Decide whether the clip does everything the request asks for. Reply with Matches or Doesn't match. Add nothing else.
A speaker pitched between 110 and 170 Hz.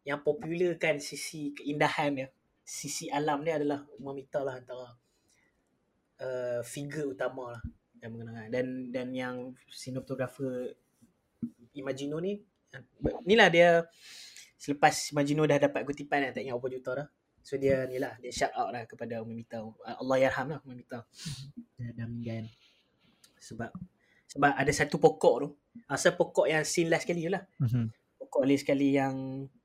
Matches